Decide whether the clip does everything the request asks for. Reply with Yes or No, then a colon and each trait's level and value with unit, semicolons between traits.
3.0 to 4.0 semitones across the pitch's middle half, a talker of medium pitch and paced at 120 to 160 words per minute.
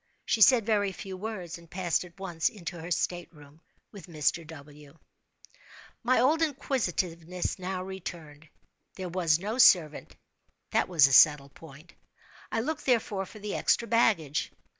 No: average, 4.6 semitones; medium, 180 Hz; average, 145 wpm